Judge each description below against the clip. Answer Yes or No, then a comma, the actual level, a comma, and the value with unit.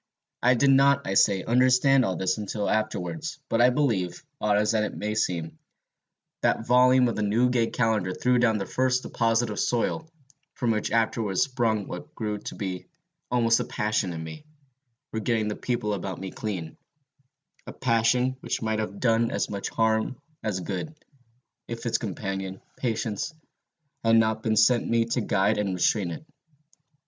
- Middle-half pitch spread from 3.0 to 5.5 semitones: Yes, average, 3.3 semitones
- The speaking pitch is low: Yes, low, 110 Hz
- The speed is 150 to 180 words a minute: Yes, average, 170 wpm